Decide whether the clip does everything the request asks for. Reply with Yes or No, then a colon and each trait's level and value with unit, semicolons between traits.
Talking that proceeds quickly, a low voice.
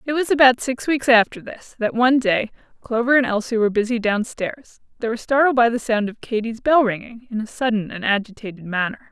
No: fast, 215 wpm; high, 230 Hz